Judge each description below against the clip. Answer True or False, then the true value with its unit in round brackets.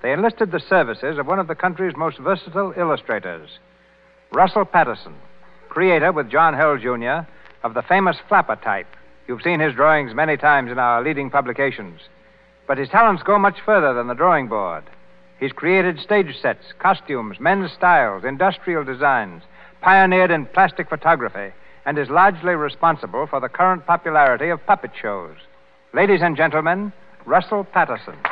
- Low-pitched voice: False (170 Hz)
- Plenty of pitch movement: False (4.4 semitones)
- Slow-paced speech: False (155 wpm)